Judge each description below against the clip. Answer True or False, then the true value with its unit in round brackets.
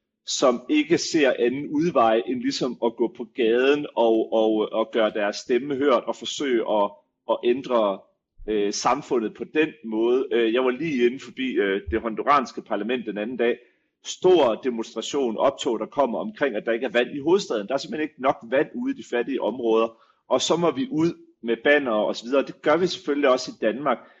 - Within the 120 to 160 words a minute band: False (200 wpm)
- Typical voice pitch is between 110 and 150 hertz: True (125 Hz)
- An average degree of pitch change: False (8.5 semitones)